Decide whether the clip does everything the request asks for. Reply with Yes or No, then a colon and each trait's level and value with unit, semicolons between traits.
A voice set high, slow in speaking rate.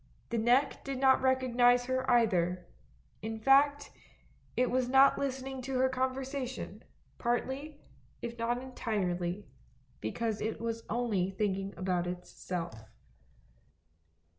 Yes: high, 240 Hz; slow, 115 wpm